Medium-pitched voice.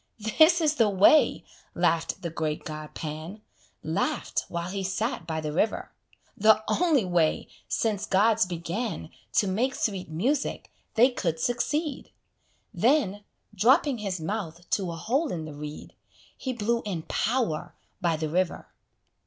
No: high, 200 Hz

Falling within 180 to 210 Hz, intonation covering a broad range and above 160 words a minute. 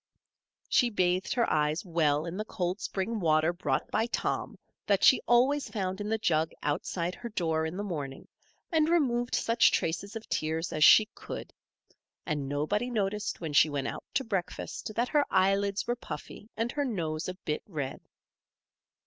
Yes: high, 190 Hz; wide, 6.1 semitones; average, 175 wpm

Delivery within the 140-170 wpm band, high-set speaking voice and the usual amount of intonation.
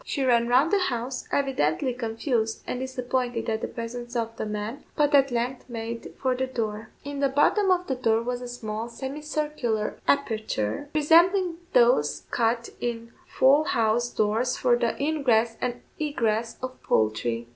Yes: average, 160 wpm; high, 245 Hz; average, 3.6 semitones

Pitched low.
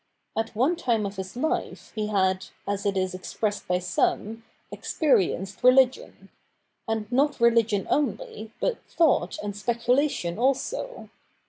No: high, 225 Hz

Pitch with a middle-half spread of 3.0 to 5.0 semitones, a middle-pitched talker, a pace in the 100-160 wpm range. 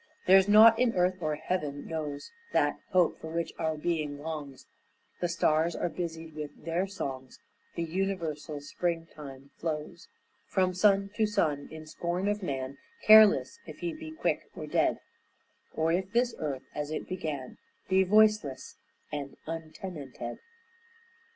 Yes: average, 4.2 semitones; medium, 165 Hz; average, 145 wpm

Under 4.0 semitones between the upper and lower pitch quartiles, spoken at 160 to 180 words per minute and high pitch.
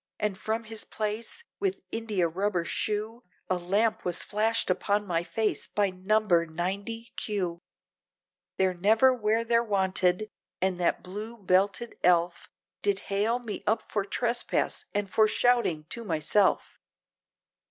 No: average, 3.4 semitones; slow, 135 wpm; high, 205 Hz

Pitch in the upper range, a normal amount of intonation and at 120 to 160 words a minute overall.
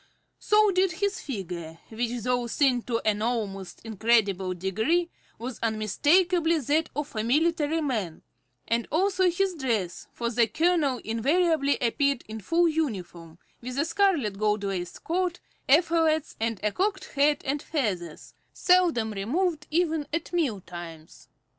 No: very high, 260 Hz; wide, 7.5 semitones; average, 140 wpm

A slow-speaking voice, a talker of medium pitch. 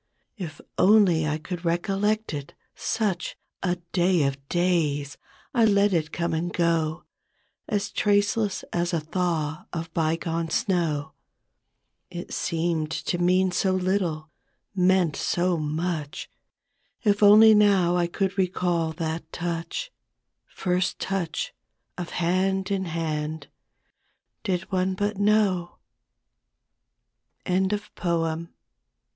Yes: slow, 115 wpm; medium, 175 Hz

